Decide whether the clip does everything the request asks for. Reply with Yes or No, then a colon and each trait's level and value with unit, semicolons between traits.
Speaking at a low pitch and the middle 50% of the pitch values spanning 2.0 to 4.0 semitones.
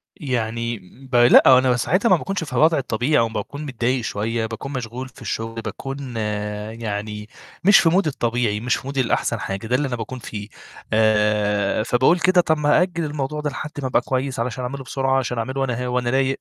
Yes: low, 125 Hz; average, 3.6 semitones